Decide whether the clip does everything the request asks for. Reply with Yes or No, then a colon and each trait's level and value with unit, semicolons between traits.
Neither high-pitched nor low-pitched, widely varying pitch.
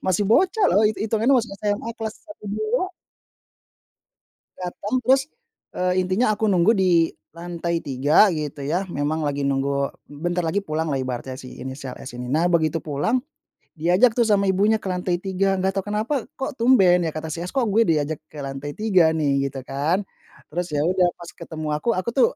Yes: medium, 180 Hz; wide, 6.0 semitones